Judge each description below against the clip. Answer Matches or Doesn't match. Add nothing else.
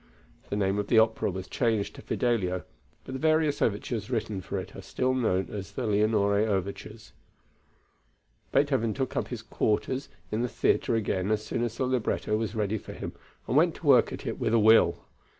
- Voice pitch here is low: Matches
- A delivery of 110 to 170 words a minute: Doesn't match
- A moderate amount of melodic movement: Matches